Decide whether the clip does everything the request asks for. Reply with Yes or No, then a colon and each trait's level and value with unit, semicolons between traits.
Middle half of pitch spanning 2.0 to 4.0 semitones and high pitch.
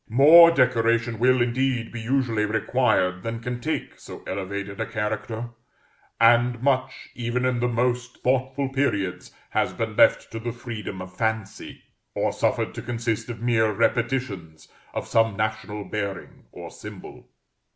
No: narrow, 2.6 semitones; low, 115 Hz